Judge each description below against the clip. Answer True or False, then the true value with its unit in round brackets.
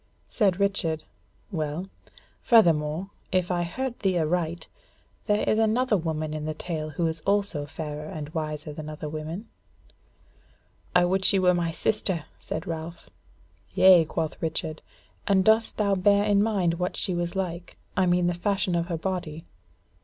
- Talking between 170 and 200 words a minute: False (160 wpm)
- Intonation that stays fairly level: False (3.5 semitones)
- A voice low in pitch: False (175 Hz)